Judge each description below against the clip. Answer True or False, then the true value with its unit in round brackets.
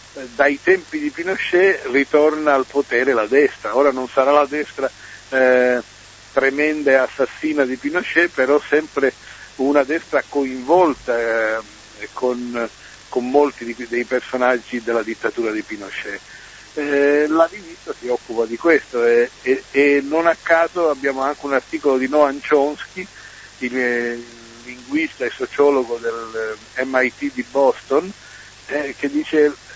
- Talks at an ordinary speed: True (140 wpm)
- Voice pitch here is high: False (140 Hz)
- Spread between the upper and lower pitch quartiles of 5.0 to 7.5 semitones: False (4.3 semitones)